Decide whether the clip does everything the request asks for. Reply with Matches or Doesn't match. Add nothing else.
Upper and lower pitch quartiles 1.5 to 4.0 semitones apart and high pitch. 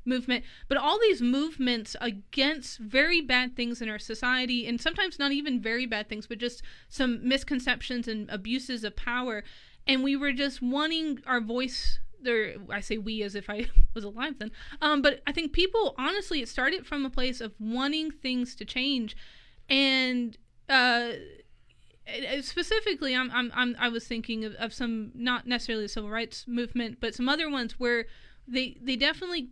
Matches